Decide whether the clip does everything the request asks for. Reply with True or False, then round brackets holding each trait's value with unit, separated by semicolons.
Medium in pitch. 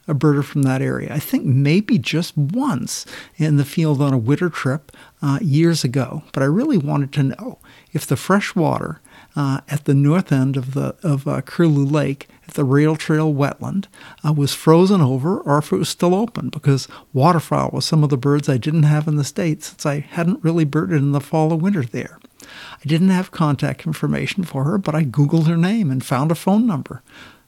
True (150 Hz)